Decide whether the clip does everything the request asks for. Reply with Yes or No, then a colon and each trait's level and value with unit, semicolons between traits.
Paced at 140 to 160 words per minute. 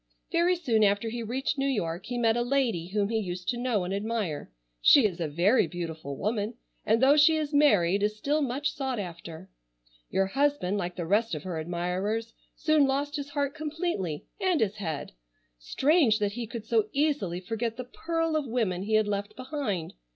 No: average, 195 wpm